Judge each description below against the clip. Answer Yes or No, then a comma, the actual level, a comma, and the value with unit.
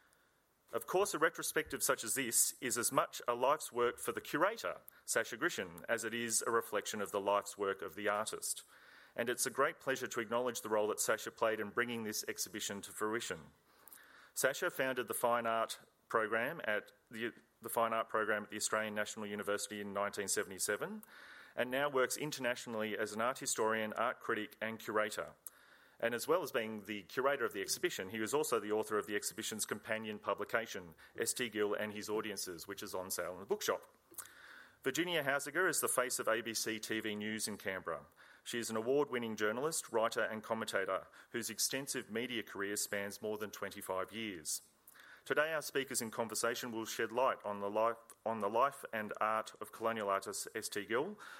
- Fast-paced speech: No, average, 185 wpm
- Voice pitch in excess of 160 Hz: No, low, 110 Hz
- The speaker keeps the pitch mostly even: Yes, narrow, 2.2 semitones